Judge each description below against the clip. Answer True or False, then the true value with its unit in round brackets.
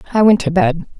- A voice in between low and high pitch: False (200 Hz)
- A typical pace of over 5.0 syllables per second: True (6.4 syllables/s)